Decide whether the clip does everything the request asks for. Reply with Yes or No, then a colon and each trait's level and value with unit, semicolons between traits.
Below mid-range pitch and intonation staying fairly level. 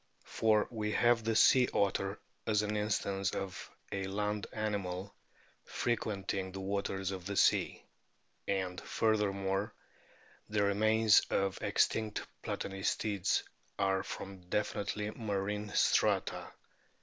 Yes: low, 100 Hz; narrow, 1.7 semitones